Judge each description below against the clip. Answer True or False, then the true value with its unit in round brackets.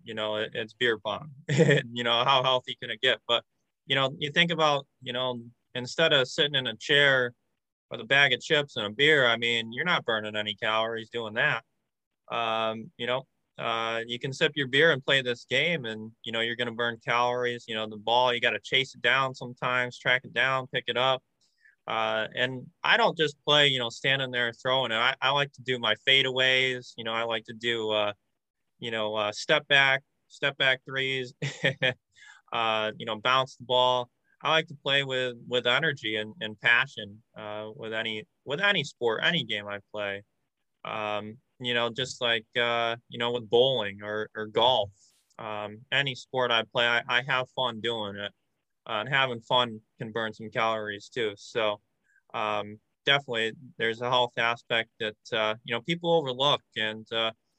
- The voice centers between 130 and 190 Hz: False (120 Hz)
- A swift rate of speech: False (195 wpm)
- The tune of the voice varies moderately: True (3.0 semitones)